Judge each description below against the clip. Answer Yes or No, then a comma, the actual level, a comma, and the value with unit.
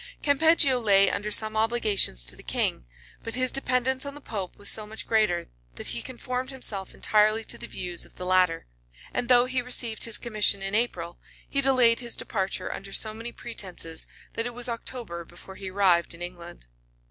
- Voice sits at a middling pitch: No, high, 215 Hz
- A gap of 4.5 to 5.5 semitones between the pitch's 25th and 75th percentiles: Yes, average, 4.8 semitones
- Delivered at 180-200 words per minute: Yes, average, 190 wpm